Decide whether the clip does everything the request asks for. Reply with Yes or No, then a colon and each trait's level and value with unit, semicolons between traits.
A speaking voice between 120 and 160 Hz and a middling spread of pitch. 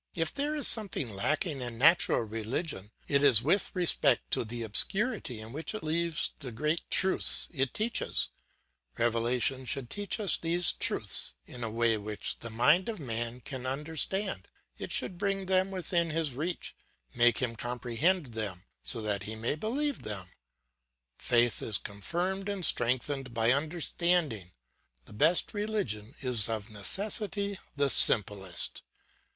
No: low, 135 Hz; wide, 7.7 semitones